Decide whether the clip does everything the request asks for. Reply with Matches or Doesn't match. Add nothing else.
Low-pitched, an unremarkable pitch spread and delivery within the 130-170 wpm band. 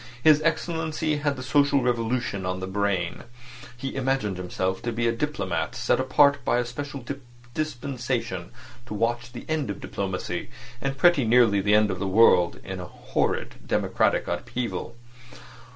Doesn't match